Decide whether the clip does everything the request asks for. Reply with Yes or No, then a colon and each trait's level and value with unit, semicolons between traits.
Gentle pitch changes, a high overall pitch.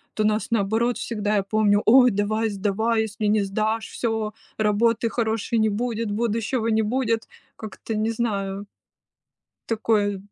Yes: narrow, 1.7 semitones; high, 220 Hz